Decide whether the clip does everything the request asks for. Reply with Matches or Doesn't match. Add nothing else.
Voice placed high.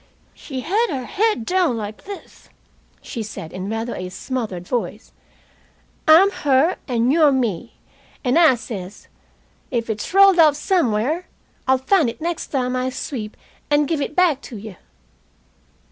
Matches